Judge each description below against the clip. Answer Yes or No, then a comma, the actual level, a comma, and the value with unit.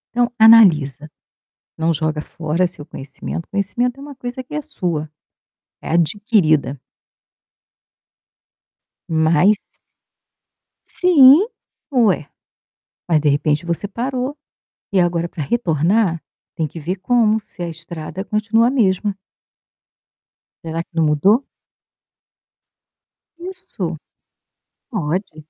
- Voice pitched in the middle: Yes, medium, 180 Hz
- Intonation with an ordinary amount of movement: No, wide, 6.4 semitones